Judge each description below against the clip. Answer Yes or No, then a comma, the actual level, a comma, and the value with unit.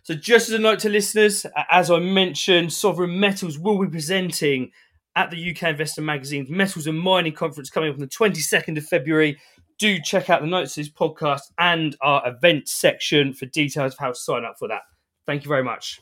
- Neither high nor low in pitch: Yes, medium, 165 Hz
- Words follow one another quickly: Yes, fast, 210 wpm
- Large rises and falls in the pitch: No, average, 4.2 semitones